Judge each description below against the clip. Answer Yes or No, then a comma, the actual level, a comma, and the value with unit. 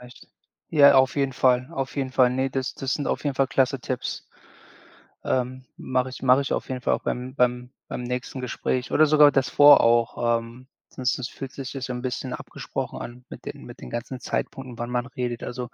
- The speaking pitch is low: Yes, low, 130 Hz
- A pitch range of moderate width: No, narrow, 1.5 semitones